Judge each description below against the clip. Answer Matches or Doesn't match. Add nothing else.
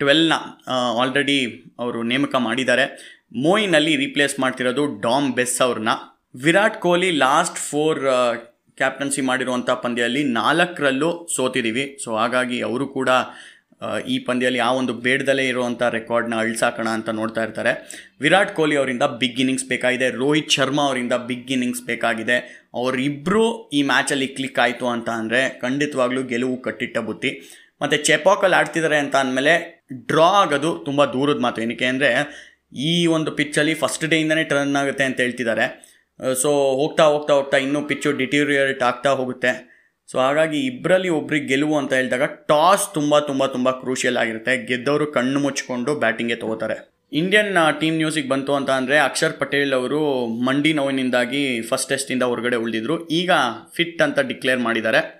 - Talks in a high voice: Doesn't match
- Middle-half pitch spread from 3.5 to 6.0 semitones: Doesn't match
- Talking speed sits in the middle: Doesn't match